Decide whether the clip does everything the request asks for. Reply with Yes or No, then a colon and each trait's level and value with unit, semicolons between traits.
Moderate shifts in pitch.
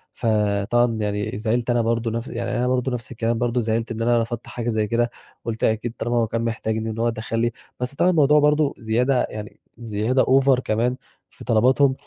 No: narrow, 1.9 semitones